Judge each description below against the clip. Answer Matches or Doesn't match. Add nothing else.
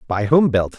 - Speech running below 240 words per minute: Matches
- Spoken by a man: Matches